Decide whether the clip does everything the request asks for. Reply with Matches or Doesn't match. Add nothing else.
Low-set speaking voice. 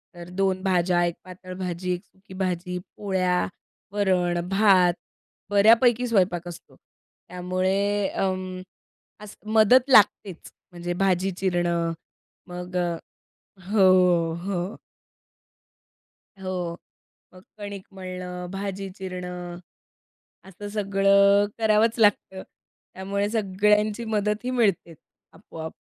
Doesn't match